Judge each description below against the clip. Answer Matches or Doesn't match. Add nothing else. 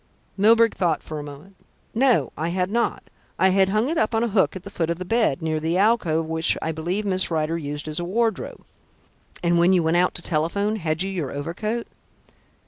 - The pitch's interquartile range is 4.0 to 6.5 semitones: Matches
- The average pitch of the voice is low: Doesn't match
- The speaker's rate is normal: Doesn't match